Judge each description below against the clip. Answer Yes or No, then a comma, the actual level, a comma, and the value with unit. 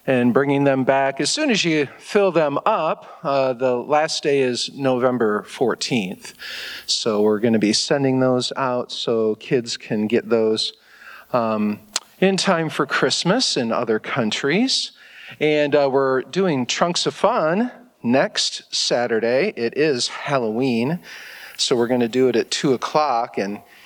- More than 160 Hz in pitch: No, low, 135 Hz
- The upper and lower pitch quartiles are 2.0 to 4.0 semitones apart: No, average, 4.8 semitones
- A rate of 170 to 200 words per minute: No, average, 155 wpm